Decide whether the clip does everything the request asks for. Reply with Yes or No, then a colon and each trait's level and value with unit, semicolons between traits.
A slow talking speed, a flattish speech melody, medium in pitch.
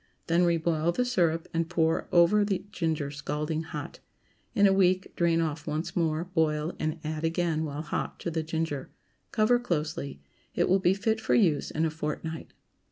No: average, 175 wpm; narrow, 2.3 semitones; medium, 165 Hz